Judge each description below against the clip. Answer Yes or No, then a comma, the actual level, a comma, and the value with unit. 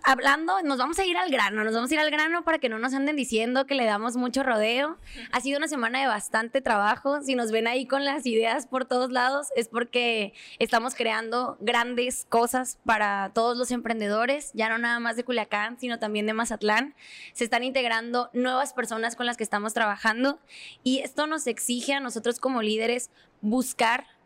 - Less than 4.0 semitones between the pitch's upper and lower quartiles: Yes, average, 2.8 semitones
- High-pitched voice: Yes, high, 245 Hz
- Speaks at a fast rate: Yes, fast, 200 wpm